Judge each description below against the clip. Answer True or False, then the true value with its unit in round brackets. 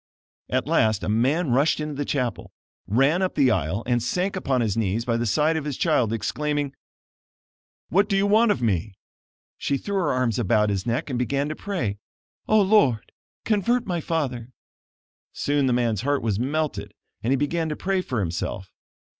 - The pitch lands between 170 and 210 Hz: False (135 Hz)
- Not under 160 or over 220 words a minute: True (185 wpm)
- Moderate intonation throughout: False (5.8 semitones)